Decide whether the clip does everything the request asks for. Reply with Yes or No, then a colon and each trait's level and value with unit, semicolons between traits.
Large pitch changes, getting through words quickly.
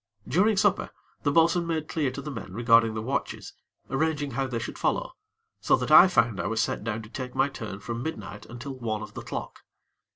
Yes: wide, 5.8 semitones; fast, 215 wpm